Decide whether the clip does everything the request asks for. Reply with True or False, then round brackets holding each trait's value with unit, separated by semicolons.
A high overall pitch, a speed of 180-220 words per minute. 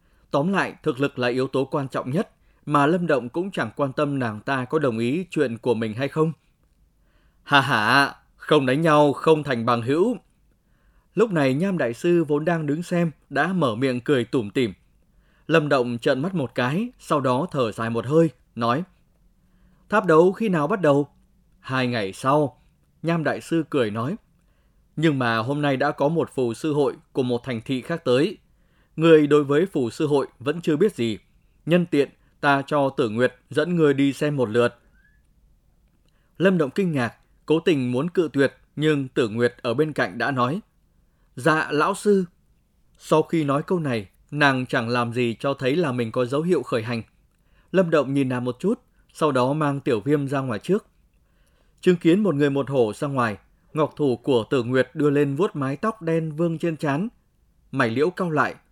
False (145 Hz; 200 wpm)